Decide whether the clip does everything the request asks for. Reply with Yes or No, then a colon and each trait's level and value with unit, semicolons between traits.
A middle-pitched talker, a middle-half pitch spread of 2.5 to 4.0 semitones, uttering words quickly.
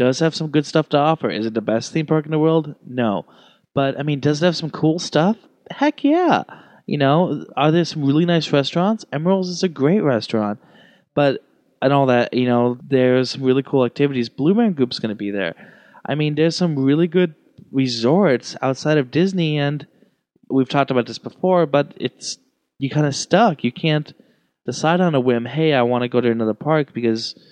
No: medium, 145 Hz; average, 4.5 semitones; fast, 210 wpm